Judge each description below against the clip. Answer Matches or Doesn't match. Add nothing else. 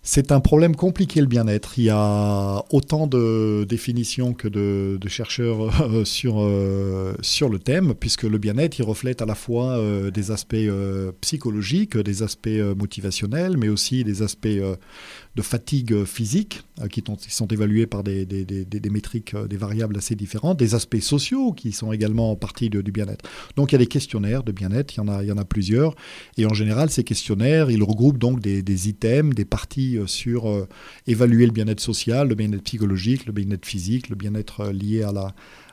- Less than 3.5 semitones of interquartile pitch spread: Matches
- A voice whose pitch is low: Matches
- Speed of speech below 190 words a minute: Doesn't match